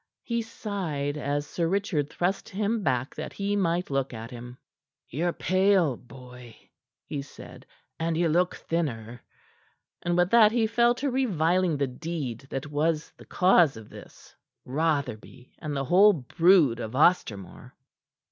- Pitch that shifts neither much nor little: No, wide, 5.9 semitones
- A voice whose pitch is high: No, medium, 160 Hz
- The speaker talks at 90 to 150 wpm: Yes, average, 145 wpm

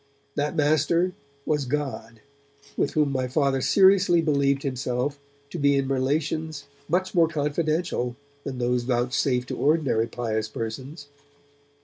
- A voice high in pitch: No, medium, 140 Hz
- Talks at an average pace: No, slow, 125 wpm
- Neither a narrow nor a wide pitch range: Yes, average, 3.7 semitones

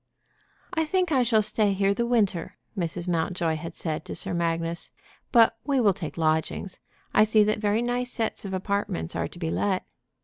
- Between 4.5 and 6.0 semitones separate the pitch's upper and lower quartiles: Yes, average, 5.1 semitones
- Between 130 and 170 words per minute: No, average, 190 wpm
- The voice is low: No, high, 200 Hz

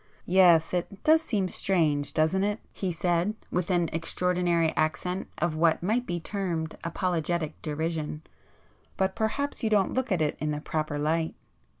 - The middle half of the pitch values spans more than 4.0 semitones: No, average, 3.2 semitones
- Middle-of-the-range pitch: Yes, medium, 175 Hz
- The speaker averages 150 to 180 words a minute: No, slow, 135 wpm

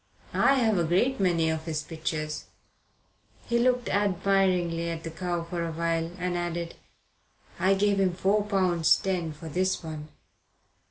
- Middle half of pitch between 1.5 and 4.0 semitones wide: Yes, average, 2.8 semitones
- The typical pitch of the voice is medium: Yes, medium, 175 Hz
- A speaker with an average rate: Yes, average, 155 wpm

